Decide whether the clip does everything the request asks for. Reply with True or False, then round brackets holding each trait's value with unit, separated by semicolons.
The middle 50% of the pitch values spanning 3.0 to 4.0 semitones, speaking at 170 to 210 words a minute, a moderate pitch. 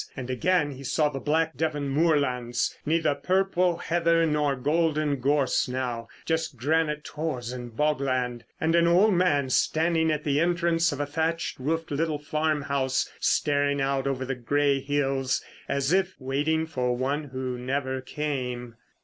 False (3.5 semitones; 150 wpm; 145 Hz)